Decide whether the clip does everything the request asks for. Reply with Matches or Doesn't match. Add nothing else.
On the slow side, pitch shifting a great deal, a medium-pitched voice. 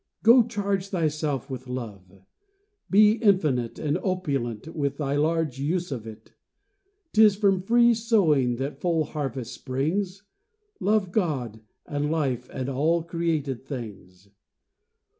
Matches